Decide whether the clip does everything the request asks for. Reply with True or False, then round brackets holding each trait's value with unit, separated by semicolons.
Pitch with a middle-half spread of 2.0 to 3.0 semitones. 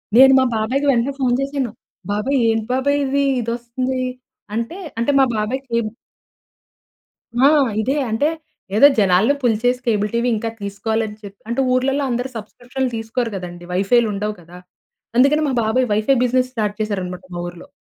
False (3.7 semitones)